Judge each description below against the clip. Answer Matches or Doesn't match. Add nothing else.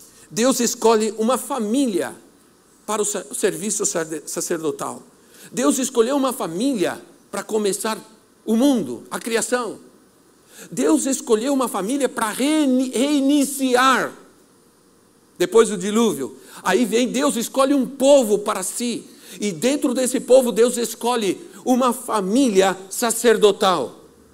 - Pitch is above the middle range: Matches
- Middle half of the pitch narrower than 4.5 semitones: Matches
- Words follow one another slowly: Matches